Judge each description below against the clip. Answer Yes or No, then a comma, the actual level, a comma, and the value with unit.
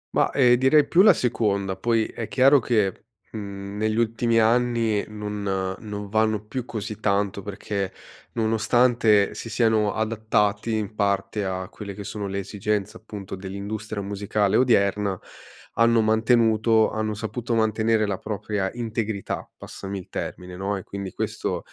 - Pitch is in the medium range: No, low, 105 Hz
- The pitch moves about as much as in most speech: No, narrow, 2.3 semitones